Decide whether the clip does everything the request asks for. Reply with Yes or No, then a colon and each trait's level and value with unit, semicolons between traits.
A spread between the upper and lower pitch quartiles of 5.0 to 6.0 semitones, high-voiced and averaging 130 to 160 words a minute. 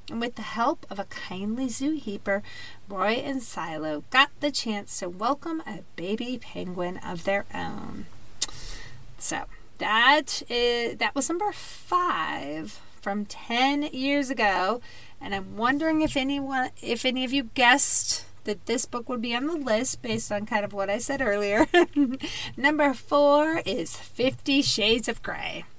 Yes: wide, 5.4 semitones; high, 240 Hz; average, 155 wpm